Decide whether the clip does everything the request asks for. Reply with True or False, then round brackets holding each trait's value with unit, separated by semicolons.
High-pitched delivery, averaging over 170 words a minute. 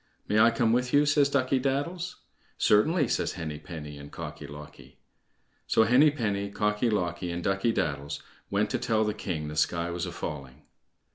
False (105 Hz; 180 wpm)